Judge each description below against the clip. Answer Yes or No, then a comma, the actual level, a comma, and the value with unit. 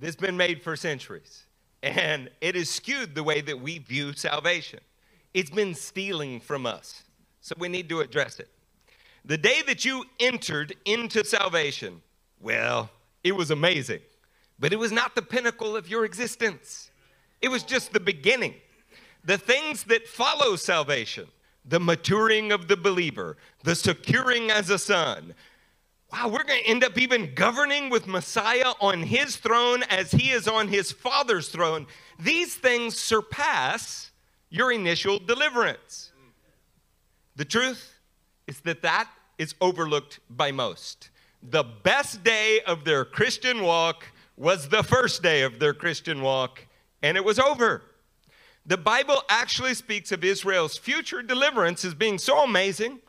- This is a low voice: No, high, 200 Hz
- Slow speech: No, average, 150 wpm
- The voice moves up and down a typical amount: No, wide, 6.0 semitones